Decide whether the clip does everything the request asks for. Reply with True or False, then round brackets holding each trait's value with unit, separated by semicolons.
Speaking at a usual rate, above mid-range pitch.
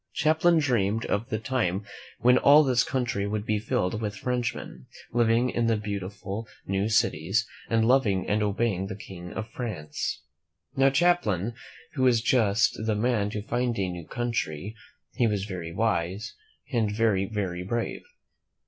False (150 wpm; 110 Hz)